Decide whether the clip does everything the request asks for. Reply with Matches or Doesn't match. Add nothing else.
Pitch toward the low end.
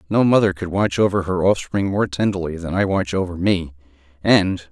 Matches